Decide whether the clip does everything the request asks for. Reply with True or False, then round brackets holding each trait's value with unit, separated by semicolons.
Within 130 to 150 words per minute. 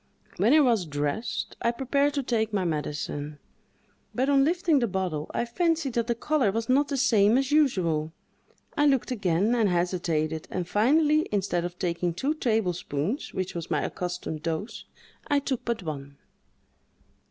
False (165 wpm)